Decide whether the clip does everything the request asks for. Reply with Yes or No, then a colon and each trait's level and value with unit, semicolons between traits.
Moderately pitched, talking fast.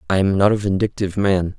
No: low, 100 Hz; fast, 225 wpm